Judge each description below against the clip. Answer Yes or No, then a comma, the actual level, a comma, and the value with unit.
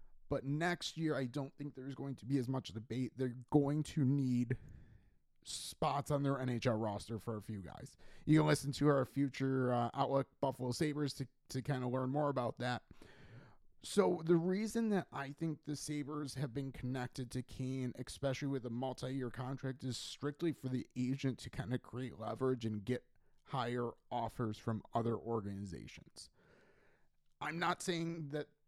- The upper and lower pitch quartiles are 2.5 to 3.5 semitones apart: Yes, average, 2.8 semitones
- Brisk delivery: No, average, 175 wpm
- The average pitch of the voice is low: Yes, low, 130 Hz